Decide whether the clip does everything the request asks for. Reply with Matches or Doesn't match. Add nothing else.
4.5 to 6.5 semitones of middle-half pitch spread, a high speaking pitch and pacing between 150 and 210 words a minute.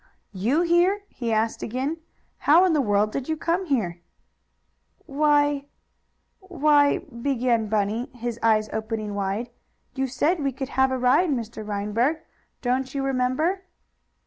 Doesn't match